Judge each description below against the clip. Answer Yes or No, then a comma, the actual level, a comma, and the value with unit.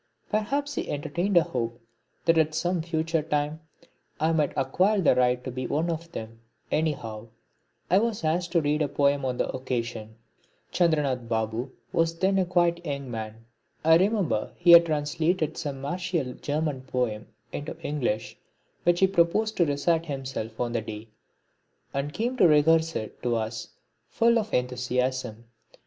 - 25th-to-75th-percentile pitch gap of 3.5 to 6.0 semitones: Yes, average, 5.3 semitones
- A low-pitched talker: No, medium, 150 Hz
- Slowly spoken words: No, average, 160 wpm